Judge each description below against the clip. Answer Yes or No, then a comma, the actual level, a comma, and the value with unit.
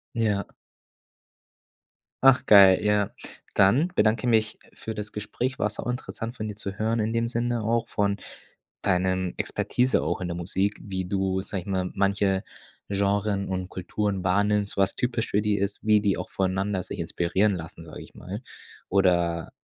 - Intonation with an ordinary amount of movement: No, narrow, 2.3 semitones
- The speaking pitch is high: No, low, 100 Hz